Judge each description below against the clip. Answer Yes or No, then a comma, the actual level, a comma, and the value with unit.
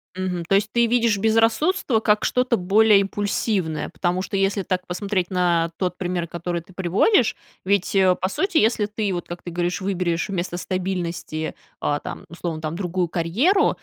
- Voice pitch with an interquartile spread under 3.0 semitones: No, average, 3.3 semitones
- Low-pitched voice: No, medium, 185 Hz